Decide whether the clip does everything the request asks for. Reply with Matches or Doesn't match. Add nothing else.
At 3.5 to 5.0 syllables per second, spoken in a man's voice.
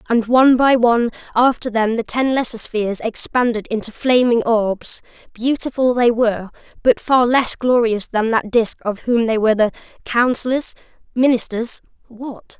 Doesn't match